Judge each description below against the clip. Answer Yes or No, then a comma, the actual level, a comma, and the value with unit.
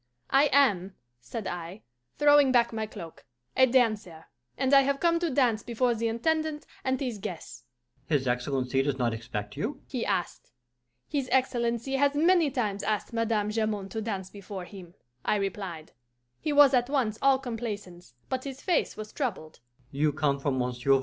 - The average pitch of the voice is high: Yes, high, 225 Hz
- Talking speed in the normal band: Yes, average, 155 wpm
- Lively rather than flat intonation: Yes, wide, 6.0 semitones